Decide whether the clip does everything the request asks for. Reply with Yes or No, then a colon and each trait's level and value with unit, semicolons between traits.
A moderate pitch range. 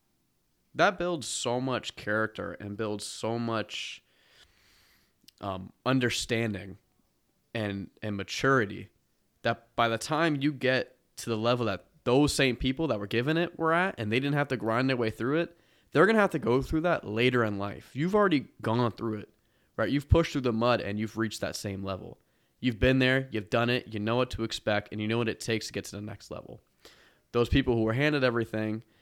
Yes: average, 3.3 semitones